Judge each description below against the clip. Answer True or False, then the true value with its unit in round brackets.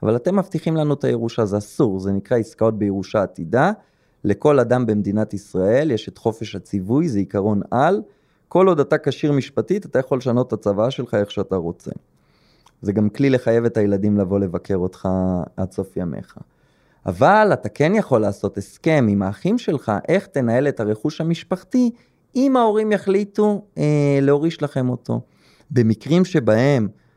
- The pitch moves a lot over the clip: True (7.4 semitones)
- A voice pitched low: True (120 Hz)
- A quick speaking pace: True (160 wpm)